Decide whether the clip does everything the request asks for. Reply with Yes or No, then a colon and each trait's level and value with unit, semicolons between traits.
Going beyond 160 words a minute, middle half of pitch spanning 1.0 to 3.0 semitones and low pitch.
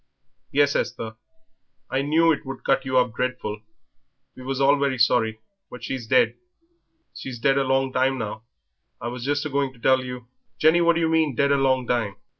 Yes: fast, 205 wpm; narrow, 2.4 semitones; low, 130 Hz